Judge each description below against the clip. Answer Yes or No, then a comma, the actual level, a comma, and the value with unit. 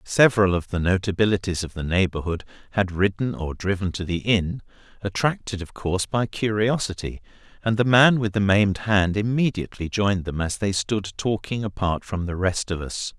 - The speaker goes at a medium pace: Yes, average, 180 wpm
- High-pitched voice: No, low, 100 Hz